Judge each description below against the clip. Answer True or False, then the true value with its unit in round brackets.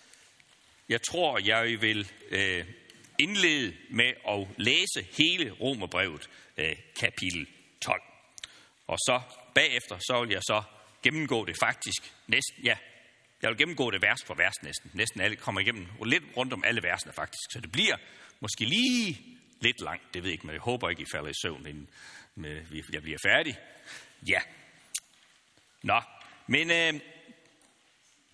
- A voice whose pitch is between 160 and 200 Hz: False (115 Hz)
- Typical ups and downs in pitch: False (8.3 semitones)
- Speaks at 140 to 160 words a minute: True (150 wpm)